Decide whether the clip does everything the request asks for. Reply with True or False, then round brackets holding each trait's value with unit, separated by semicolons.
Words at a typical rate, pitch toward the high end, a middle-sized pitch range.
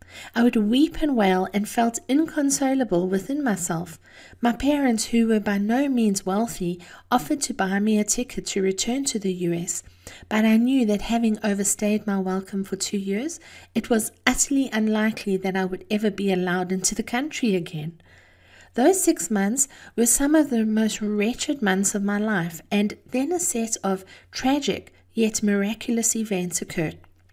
True (170 wpm; 215 Hz; 4.1 semitones)